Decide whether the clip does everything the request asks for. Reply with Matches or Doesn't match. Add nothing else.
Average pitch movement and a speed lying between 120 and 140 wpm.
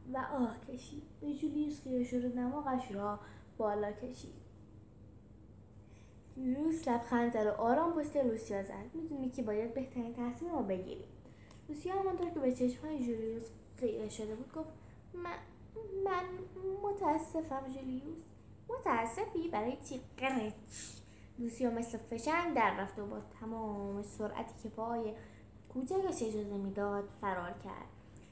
Doesn't match